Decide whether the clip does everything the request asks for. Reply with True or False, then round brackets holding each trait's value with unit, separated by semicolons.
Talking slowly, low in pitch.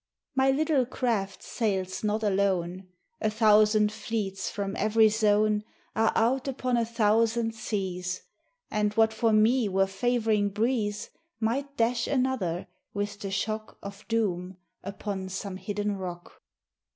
False (130 wpm; 215 Hz)